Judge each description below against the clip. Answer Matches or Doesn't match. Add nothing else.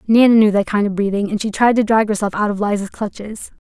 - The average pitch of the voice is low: Doesn't match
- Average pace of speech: Doesn't match